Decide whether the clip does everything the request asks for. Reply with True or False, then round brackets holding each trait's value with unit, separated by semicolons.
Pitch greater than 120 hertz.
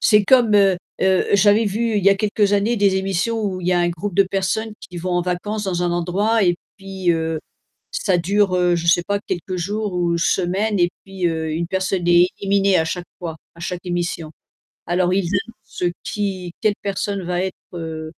True (185 Hz)